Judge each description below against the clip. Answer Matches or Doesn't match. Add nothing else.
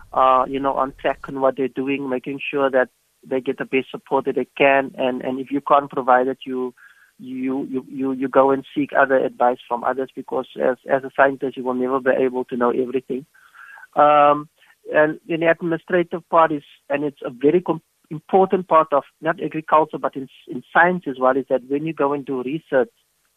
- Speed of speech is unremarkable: Doesn't match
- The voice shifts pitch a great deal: Doesn't match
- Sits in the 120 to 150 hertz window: Matches